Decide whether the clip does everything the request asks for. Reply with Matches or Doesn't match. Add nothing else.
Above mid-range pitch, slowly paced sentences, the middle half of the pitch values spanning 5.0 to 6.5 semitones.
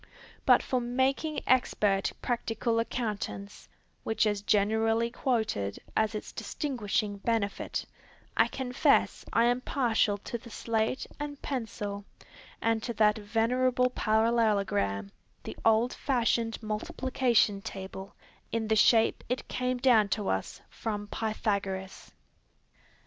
Doesn't match